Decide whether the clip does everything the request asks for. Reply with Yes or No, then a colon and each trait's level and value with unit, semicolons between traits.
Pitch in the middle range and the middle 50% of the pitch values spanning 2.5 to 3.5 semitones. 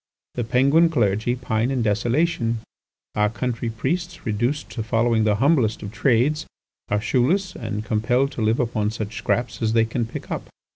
No: low, 115 Hz; average, 3.0 semitones